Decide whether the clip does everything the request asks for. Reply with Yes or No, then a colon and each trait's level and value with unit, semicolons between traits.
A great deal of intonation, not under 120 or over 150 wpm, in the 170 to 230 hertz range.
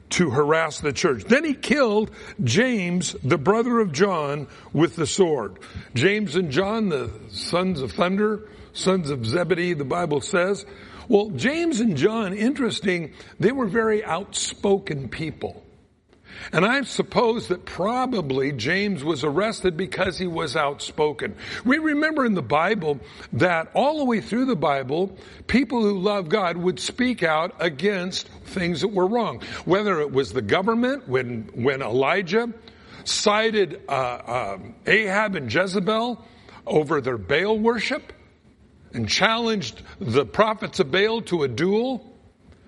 Yes: wide, 5.7 semitones; average, 140 wpm; high, 190 Hz